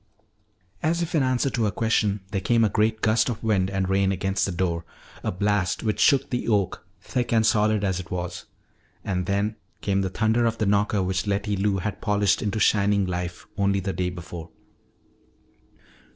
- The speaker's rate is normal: Yes, average, 190 wpm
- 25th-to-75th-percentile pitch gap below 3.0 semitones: Yes, narrow, 2.6 semitones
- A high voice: No, low, 100 Hz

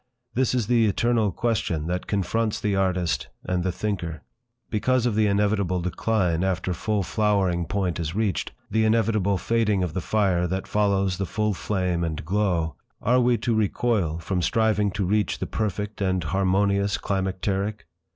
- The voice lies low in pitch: Yes, low, 100 Hz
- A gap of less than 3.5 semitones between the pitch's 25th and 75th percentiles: Yes, average, 2.9 semitones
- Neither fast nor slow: Yes, average, 160 wpm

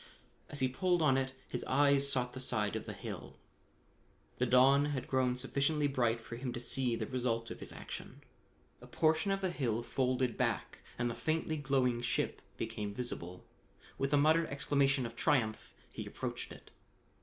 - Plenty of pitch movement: No, average, 3.0 semitones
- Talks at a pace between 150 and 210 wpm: Yes, average, 180 wpm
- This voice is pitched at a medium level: No, low, 130 Hz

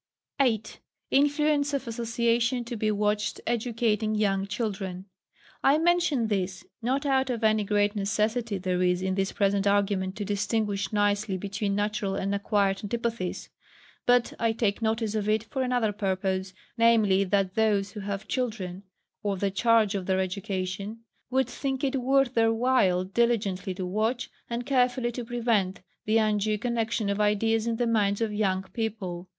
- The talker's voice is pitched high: Yes, high, 215 Hz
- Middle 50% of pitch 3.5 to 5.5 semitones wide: No, average, 3.0 semitones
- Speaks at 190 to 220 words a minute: No, average, 160 wpm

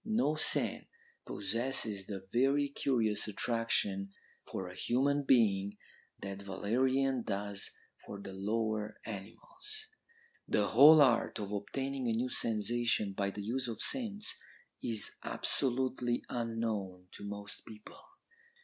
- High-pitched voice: No, low, 115 Hz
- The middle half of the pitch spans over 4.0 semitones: Yes, average, 4.6 semitones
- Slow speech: Yes, slow, 120 wpm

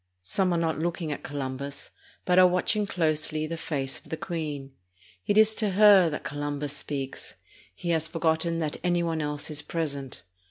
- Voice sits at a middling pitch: Yes, medium, 160 Hz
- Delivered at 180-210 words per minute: Yes, average, 185 wpm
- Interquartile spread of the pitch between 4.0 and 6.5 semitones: No, average, 3.1 semitones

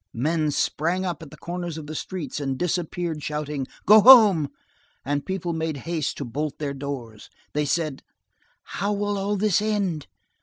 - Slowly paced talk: No, average, 165 wpm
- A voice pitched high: No, medium, 160 Hz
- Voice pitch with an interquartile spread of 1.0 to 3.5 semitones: No, average, 4.3 semitones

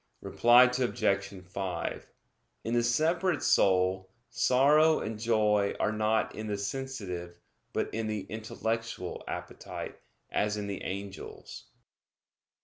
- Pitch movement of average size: Yes, average, 3.2 semitones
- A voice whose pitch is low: Yes, low, 110 Hz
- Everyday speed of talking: No, slow, 115 wpm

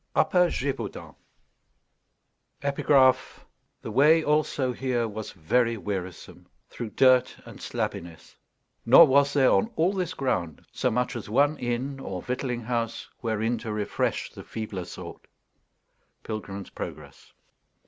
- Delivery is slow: Yes, slow, 120 wpm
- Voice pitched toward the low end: Yes, low, 120 Hz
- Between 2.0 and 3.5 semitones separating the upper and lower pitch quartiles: No, average, 4.3 semitones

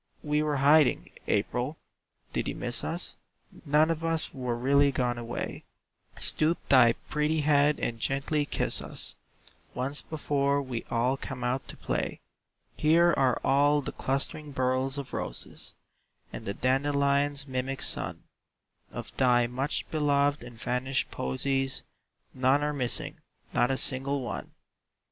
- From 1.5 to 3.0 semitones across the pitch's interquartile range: Yes, narrow, 2.4 semitones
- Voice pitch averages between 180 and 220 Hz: No, low, 135 Hz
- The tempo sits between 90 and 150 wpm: Yes, average, 140 wpm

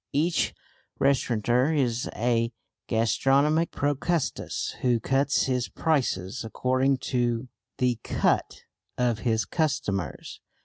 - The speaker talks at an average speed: No, slow, 95 wpm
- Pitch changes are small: No, average, 3.2 semitones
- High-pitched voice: No, low, 125 Hz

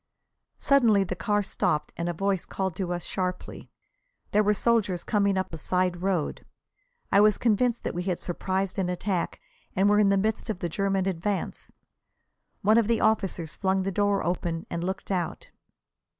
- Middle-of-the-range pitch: No, high, 195 Hz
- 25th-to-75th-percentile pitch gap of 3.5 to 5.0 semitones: No, narrow, 2.5 semitones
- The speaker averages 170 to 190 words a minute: Yes, average, 180 wpm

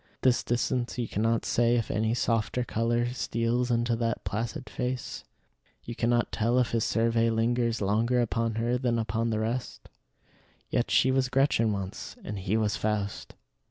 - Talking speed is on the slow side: No, average, 165 wpm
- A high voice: No, low, 115 Hz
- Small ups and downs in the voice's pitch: Yes, narrow, 1.6 semitones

